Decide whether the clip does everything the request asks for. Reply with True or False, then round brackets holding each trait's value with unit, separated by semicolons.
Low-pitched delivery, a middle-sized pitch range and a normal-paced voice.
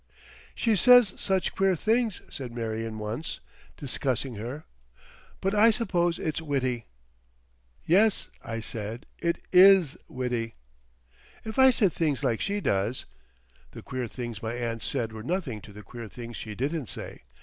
False (130 Hz; 8.6 semitones; 150 wpm)